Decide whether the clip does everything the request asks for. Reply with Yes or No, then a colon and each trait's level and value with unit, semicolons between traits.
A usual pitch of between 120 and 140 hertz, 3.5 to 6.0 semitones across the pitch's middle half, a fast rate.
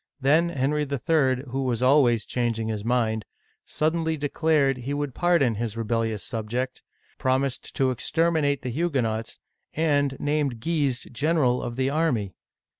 No: low, 135 Hz; average, 4.1 semitones; average, 150 wpm